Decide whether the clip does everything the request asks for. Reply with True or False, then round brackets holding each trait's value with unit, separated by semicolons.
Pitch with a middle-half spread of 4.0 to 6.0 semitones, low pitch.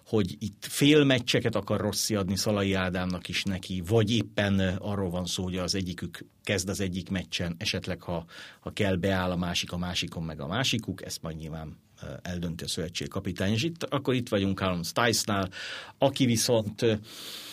False (3.1 semitones; 95 Hz)